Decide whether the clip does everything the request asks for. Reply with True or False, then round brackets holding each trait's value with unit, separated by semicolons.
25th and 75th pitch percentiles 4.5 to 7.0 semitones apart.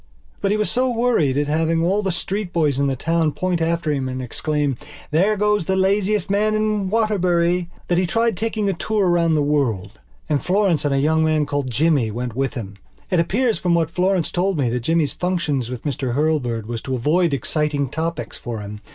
True (5.3 semitones)